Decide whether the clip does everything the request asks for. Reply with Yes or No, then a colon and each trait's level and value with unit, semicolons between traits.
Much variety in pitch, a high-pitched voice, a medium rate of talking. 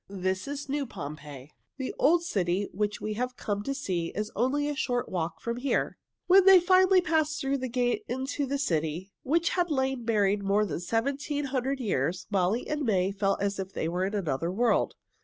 Yes: wide, 6.7 semitones; high, 235 Hz; average, 195 wpm